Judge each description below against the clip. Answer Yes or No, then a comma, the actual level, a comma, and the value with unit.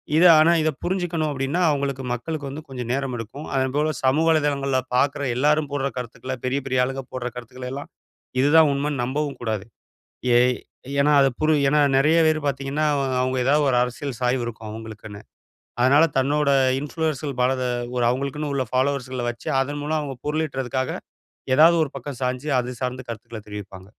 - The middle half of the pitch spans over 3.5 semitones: No, average, 2.8 semitones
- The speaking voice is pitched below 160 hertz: Yes, low, 135 Hz